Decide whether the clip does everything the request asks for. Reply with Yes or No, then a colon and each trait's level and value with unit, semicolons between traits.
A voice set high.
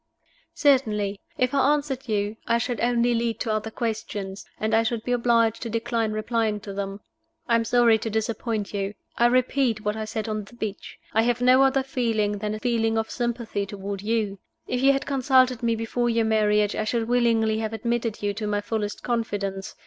Yes: high, 225 Hz